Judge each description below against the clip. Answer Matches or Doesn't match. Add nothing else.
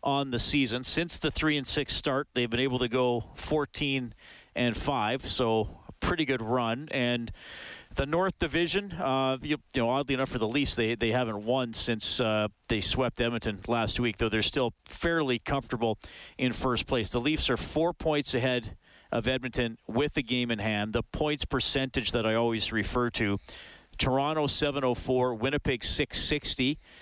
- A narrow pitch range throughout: Doesn't match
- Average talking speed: Matches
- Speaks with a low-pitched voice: Matches